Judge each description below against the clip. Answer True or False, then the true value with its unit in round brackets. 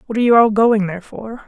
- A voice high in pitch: True (215 Hz)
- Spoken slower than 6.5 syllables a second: False (6.9 syllables/s)